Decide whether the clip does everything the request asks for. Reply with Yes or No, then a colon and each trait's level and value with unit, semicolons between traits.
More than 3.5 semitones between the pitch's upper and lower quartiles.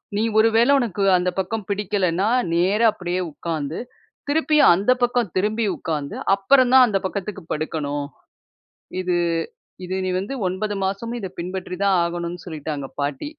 Yes: average, 4.2 semitones